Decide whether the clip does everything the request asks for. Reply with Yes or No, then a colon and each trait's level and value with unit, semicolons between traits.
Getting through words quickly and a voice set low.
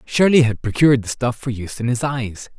Yes: fast, 230 wpm; low, 120 Hz